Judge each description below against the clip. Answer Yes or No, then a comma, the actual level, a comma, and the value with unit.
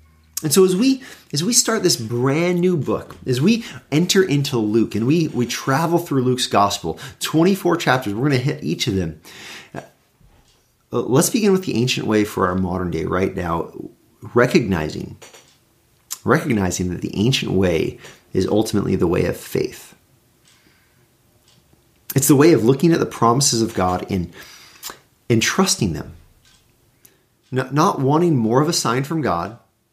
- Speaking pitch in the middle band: No, low, 125 Hz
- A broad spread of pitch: Yes, wide, 7.2 semitones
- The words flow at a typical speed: Yes, average, 160 wpm